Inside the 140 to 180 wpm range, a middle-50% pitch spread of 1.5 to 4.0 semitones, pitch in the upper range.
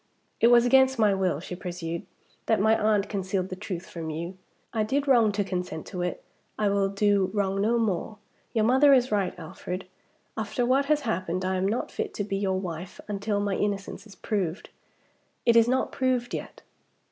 No: average, 195 wpm; average, 3.6 semitones; high, 200 Hz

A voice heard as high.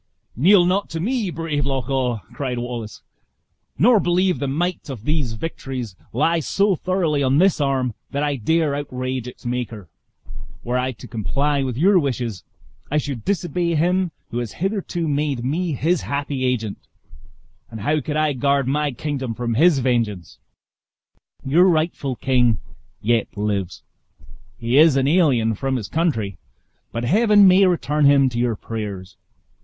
No: medium, 140 Hz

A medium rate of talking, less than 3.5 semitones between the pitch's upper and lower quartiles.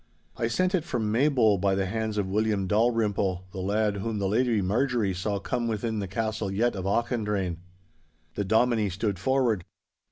Yes: average, 170 wpm; average, 2.9 semitones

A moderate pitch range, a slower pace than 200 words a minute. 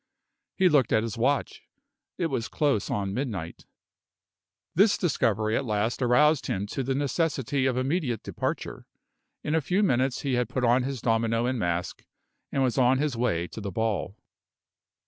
Yes: average, 4.0 semitones; average, 165 wpm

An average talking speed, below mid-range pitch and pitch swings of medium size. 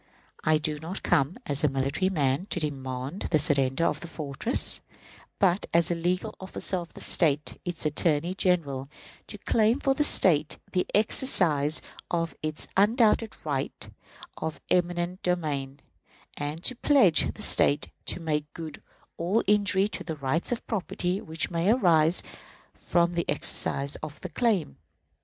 No: average, 150 wpm; medium, 165 Hz; average, 4.1 semitones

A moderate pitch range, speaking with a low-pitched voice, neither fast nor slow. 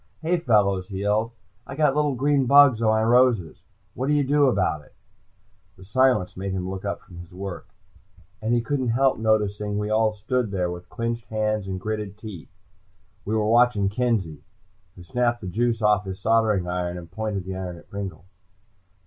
Yes: average, 4.1 semitones; low, 105 Hz; average, 190 wpm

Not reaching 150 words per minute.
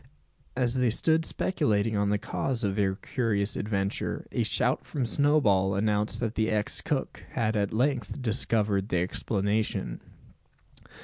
Yes: average, 140 wpm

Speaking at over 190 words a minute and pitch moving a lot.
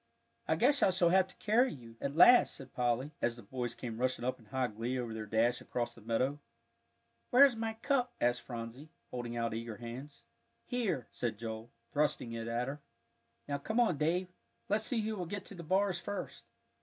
Yes: average, 200 wpm; wide, 8.2 semitones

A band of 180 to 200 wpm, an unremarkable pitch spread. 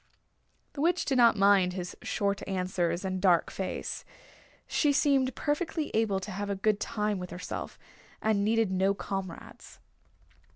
No: average, 150 wpm; average, 3.3 semitones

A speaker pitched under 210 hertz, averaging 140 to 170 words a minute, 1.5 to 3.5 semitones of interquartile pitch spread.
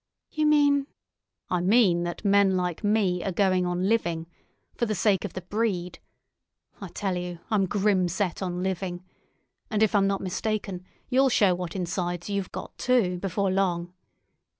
Yes: high, 190 Hz; average, 160 wpm; average, 2.8 semitones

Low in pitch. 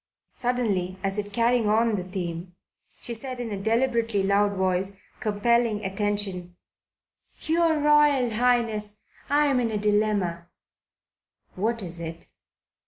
No: high, 210 Hz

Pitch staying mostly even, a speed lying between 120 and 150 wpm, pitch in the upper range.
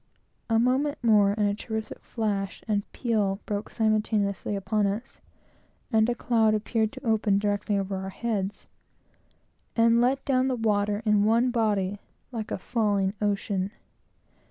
Yes: narrow, 2.2 semitones; average, 145 wpm; high, 215 Hz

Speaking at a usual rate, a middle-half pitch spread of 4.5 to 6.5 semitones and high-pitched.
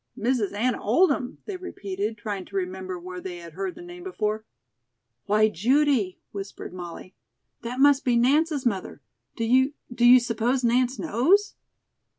Yes: average, 155 wpm; average, 5.2 semitones; high, 235 Hz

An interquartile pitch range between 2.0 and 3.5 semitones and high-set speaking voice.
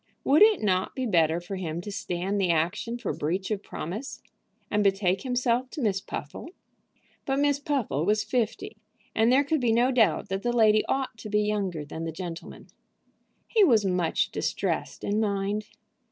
No: average, 4.8 semitones; high, 210 Hz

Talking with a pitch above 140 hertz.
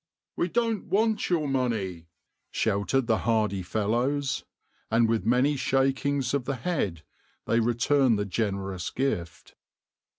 No: low, 120 Hz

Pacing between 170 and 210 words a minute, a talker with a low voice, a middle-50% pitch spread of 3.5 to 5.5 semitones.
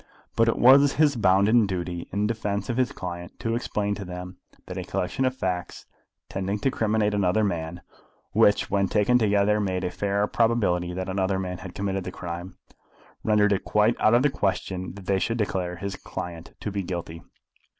No: average, 190 wpm; low, 100 Hz; average, 2.9 semitones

